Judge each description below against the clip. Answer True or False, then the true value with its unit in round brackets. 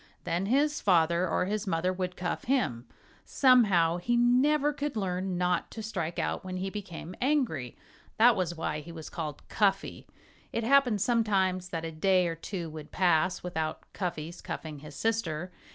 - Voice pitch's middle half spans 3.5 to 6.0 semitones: True (5.1 semitones)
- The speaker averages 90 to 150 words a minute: False (170 wpm)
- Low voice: False (185 Hz)